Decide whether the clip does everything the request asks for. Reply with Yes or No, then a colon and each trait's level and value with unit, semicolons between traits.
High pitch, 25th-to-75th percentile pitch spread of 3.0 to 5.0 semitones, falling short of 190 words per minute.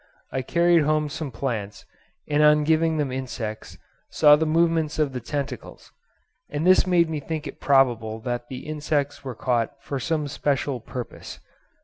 No: medium, 145 Hz; average, 3.3 semitones; average, 160 wpm